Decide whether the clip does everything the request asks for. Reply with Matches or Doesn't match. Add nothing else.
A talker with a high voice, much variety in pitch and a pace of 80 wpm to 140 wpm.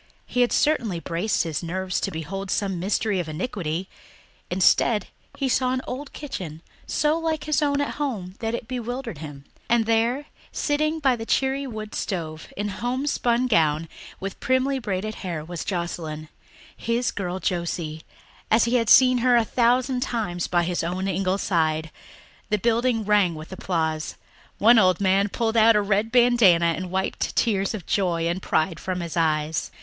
Doesn't match